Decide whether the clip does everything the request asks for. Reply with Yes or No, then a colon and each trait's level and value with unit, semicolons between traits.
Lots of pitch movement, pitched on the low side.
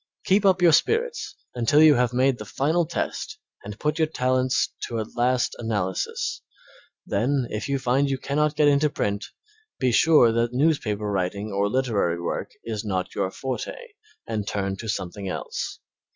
Yes: wide, 6.0 semitones; low, 125 Hz